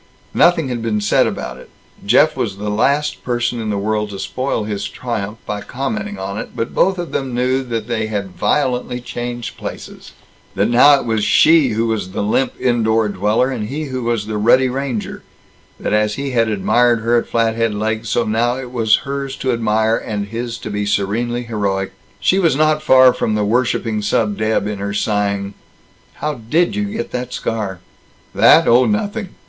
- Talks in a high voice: No, low, 115 Hz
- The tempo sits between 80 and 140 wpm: No, average, 190 wpm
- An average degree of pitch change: Yes, average, 3.4 semitones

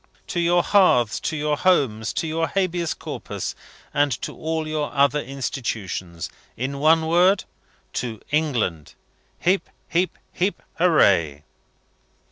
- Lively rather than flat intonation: Yes, wide, 6.1 semitones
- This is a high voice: No, medium, 150 Hz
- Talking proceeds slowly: Yes, slow, 120 wpm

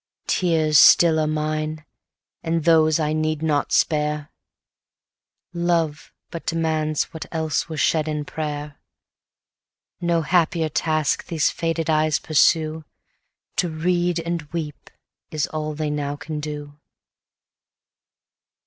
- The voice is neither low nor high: Yes, medium, 155 Hz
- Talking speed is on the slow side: Yes, slow, 115 wpm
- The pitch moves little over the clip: Yes, narrow, 1.4 semitones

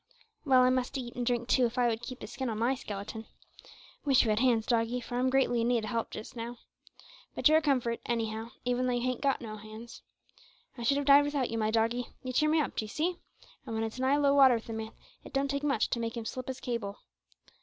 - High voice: Yes, high, 245 Hz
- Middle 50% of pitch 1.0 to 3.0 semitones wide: Yes, narrow, 2.5 semitones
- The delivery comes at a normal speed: No, fast, 255 wpm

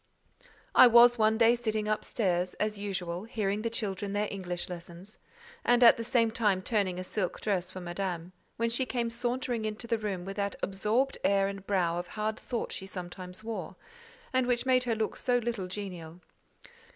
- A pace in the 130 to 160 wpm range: No, average, 190 wpm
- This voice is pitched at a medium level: No, high, 210 Hz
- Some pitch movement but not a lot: Yes, average, 3.8 semitones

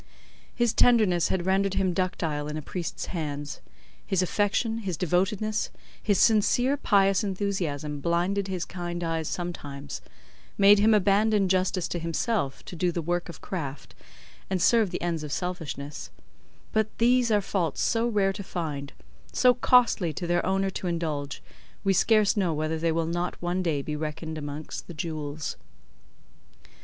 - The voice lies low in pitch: No, medium, 180 Hz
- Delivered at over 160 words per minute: No, average, 155 wpm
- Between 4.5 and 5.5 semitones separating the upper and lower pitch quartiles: No, average, 3.9 semitones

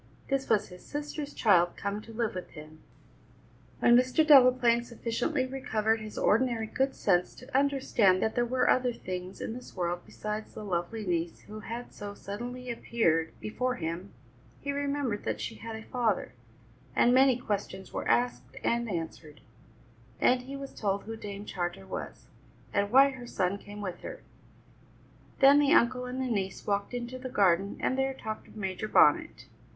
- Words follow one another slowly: No, average, 170 wpm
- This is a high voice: Yes, high, 220 Hz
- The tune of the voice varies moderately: Yes, average, 4.8 semitones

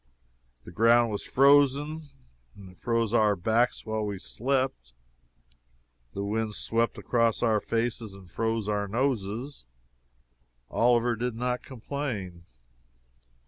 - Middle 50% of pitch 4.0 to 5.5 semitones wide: No, average, 3.0 semitones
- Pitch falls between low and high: No, low, 115 Hz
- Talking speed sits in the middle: No, slow, 115 wpm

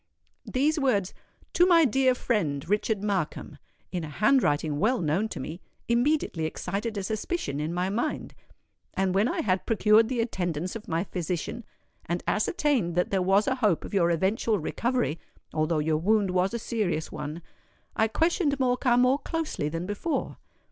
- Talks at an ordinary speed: Yes, average, 160 wpm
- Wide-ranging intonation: Yes, wide, 6.2 semitones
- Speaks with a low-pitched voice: No, high, 205 Hz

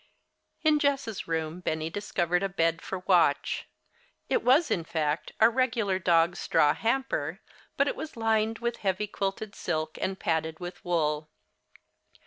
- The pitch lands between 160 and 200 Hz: Yes, medium, 185 Hz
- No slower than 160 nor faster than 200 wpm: No, average, 145 wpm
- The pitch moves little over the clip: No, wide, 5.5 semitones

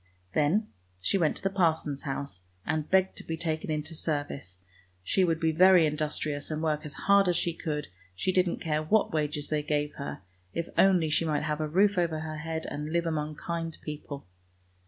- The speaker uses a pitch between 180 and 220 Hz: No, medium, 155 Hz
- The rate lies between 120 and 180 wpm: No, average, 200 wpm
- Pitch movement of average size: No, narrow, 2.2 semitones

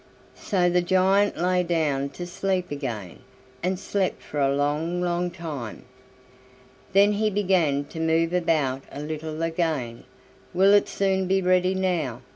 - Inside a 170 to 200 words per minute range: No, average, 145 wpm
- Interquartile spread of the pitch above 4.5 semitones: No, average, 4.0 semitones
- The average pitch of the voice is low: No, medium, 175 Hz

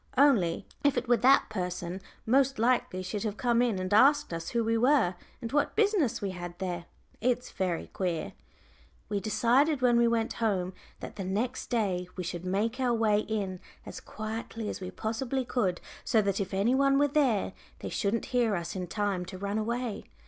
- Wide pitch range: No, average, 4.8 semitones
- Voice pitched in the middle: No, high, 220 Hz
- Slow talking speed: No, average, 190 wpm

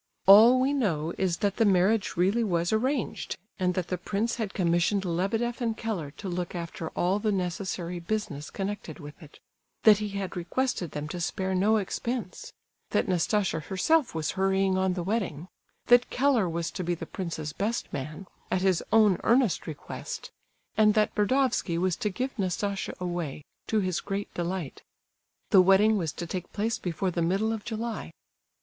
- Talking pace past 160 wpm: Yes, average, 175 wpm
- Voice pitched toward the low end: No, high, 190 Hz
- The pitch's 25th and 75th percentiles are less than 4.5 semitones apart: Yes, average, 3.9 semitones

